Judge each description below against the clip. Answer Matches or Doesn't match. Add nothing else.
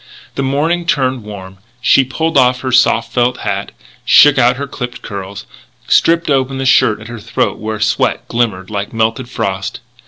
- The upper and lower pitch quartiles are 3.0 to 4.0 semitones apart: Matches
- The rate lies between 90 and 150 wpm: Doesn't match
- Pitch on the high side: Doesn't match